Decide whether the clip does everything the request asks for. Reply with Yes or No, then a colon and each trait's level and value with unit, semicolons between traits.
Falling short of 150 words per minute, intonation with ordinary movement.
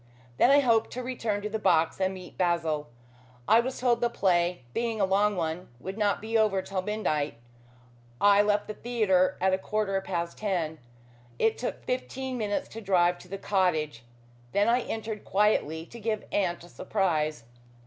No: average, 180 wpm; average, 3.9 semitones